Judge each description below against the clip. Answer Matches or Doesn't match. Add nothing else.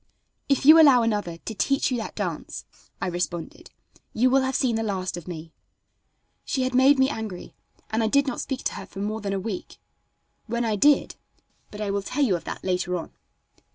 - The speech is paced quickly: Matches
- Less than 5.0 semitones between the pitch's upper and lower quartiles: Doesn't match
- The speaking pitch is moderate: Doesn't match